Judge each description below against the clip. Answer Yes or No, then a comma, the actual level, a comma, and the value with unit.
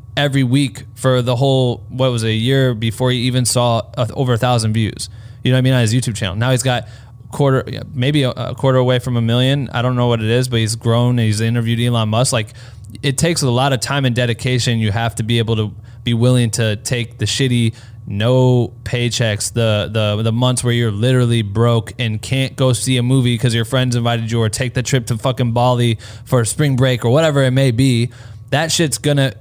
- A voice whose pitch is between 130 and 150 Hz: No, low, 120 Hz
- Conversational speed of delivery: No, fast, 230 wpm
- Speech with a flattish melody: Yes, narrow, 2.0 semitones